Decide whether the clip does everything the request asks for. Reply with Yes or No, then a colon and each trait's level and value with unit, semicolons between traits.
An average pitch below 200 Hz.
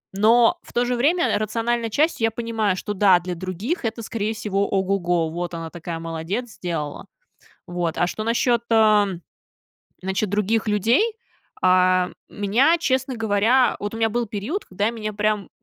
No: high, 210 Hz